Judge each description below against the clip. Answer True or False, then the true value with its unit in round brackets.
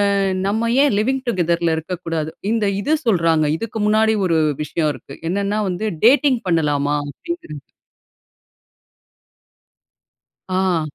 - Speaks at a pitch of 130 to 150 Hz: False (185 Hz)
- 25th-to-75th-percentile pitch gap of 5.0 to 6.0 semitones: True (5.4 semitones)